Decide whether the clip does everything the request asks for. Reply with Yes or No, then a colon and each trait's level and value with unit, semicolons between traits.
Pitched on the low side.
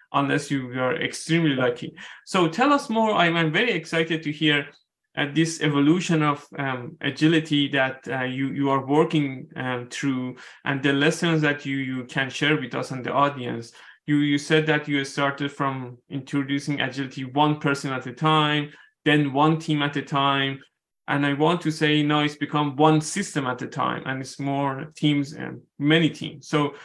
No: medium, 145 Hz